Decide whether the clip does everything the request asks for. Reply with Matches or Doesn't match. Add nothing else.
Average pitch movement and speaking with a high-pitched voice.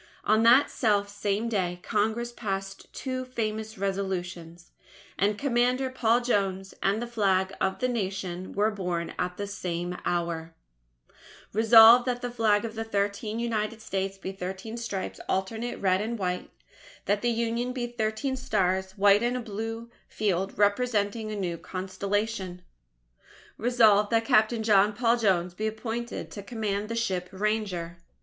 Matches